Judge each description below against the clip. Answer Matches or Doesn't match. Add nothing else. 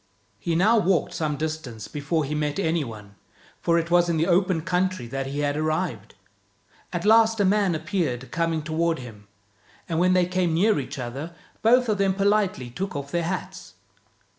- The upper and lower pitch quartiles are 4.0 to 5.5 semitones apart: Matches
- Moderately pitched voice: Matches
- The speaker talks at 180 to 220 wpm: Matches